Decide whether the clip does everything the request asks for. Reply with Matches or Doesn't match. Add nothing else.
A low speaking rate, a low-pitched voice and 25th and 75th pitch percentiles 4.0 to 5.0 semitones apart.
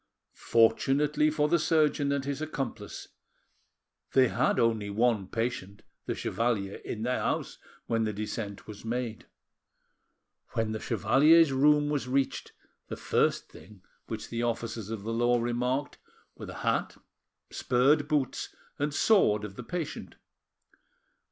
Matches